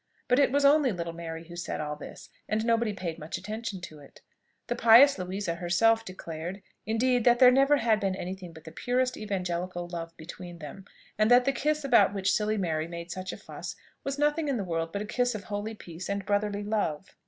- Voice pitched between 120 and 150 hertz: No, high, 200 Hz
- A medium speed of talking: No, fast, 220 wpm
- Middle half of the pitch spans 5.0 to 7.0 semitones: Yes, wide, 5.4 semitones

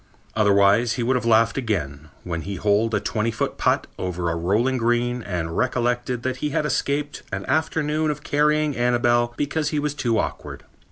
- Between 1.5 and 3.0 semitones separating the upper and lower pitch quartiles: No, wide, 5.6 semitones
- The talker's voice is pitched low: Yes, low, 120 Hz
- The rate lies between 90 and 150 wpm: No, average, 180 wpm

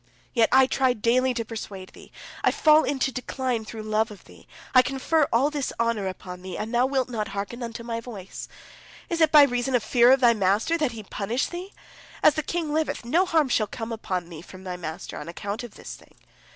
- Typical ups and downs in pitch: Yes, average, 4.2 semitones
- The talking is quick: Yes, fast, 220 wpm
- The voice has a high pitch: Yes, high, 235 Hz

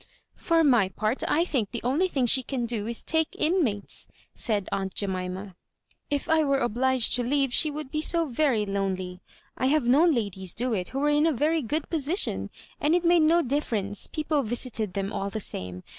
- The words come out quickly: Yes, fast, 215 wpm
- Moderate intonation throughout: No, wide, 6.9 semitones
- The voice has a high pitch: Yes, very high, 255 Hz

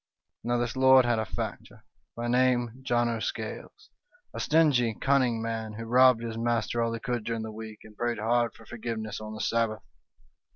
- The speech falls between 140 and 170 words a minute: No, average, 190 wpm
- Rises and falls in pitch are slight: Yes, narrow, 1.5 semitones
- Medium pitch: No, low, 115 Hz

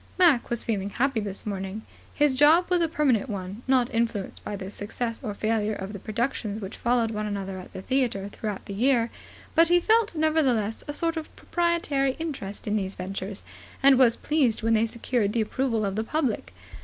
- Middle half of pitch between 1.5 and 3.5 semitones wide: No, average, 5.2 semitones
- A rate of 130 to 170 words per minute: No, average, 195 wpm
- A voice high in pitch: Yes, high, 230 Hz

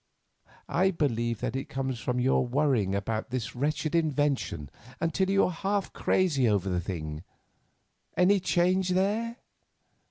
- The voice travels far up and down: Yes, wide, 8.1 semitones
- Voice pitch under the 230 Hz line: Yes, medium, 140 Hz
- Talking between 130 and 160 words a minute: Yes, slow, 135 wpm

